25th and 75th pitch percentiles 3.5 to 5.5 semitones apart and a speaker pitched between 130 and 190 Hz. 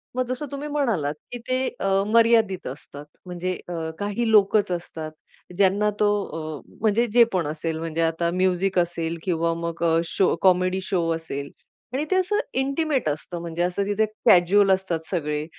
Yes: average, 4.6 semitones; medium, 185 Hz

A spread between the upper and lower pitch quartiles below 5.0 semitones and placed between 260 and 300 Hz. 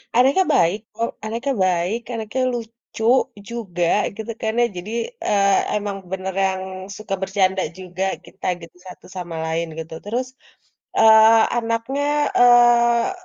No: average, 3.9 semitones; high, 215 Hz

